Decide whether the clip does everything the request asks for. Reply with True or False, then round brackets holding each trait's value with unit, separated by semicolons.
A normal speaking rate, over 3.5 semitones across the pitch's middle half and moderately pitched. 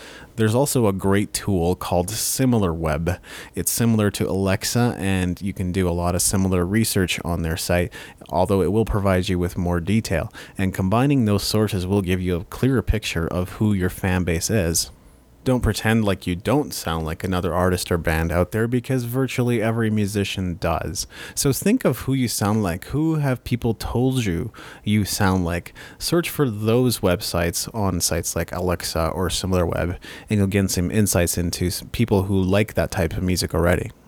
False (185 wpm; 4.1 semitones; 95 Hz)